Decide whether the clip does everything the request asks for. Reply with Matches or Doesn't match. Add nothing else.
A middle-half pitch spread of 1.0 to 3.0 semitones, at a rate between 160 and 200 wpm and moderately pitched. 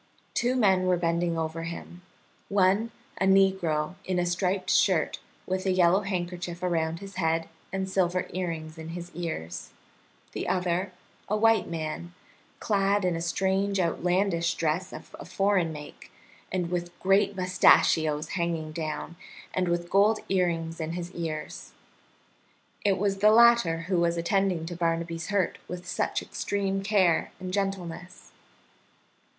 Doesn't match